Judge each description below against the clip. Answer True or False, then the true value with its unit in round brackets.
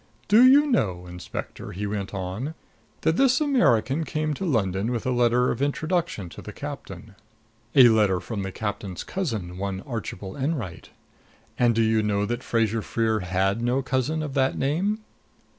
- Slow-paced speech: False (165 wpm)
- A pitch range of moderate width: False (6.6 semitones)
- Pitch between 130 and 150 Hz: False (115 Hz)